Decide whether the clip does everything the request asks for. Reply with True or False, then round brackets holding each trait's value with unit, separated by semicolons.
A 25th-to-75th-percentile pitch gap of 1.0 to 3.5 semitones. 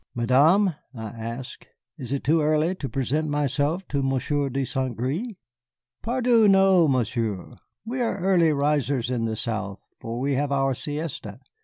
False (4.9 semitones)